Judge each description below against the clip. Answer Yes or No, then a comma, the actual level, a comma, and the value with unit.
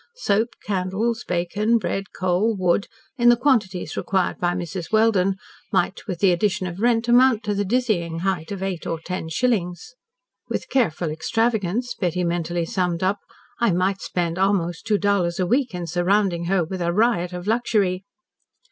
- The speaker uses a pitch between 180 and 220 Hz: Yes, high, 190 Hz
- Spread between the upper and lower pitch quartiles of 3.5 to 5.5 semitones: Yes, average, 4.0 semitones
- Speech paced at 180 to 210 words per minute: No, average, 165 wpm